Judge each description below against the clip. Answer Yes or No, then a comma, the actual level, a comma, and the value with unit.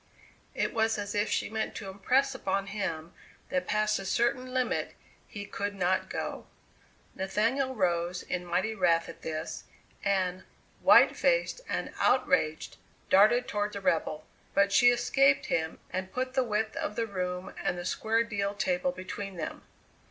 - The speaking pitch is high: Yes, high, 200 Hz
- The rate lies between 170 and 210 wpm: No, average, 160 wpm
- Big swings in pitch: No, average, 3.8 semitones